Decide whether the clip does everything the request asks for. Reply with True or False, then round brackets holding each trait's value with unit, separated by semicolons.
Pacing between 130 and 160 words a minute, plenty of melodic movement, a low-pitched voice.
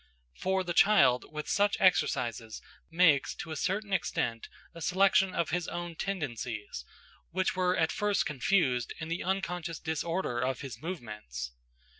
False (145 wpm; 6.8 semitones; 165 Hz)